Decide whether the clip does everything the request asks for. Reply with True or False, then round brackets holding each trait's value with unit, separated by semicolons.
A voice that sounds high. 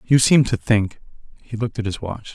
False (110 Hz)